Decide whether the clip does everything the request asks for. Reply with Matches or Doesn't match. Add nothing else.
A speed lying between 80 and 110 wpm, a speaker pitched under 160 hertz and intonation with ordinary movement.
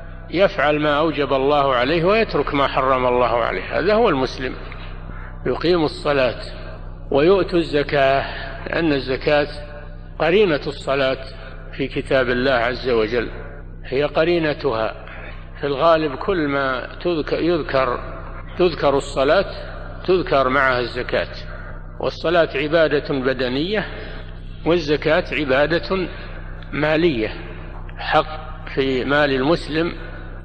Doesn't match